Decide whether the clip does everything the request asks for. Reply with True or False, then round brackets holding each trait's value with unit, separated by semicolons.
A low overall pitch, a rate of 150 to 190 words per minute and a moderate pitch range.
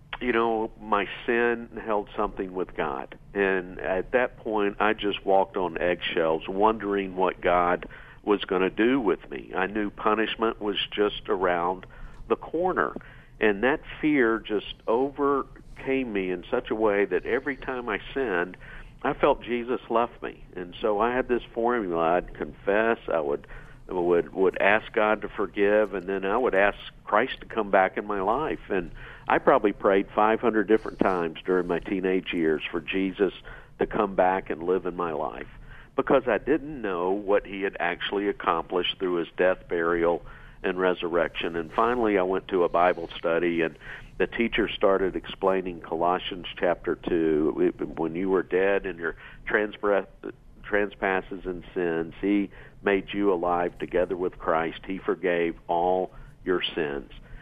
True (100 Hz; 160 wpm; 3.3 semitones)